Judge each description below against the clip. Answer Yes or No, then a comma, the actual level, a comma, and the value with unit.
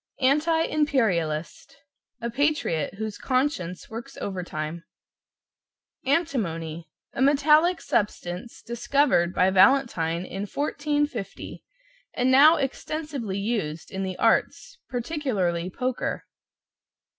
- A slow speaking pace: Yes, slow, 90 wpm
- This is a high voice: Yes, high, 235 Hz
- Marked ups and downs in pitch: Yes, wide, 8.0 semitones